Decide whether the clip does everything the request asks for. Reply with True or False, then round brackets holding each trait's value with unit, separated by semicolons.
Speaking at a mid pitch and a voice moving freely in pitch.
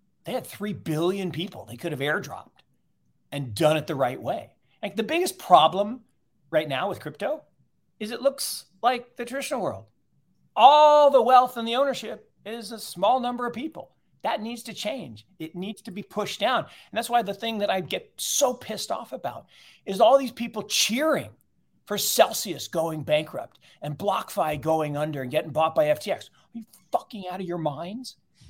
False (210 Hz; 7.1 semitones)